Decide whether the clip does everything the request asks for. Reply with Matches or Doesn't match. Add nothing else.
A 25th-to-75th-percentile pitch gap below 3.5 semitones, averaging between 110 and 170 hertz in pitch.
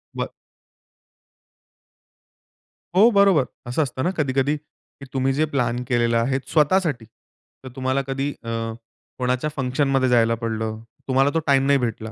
Matches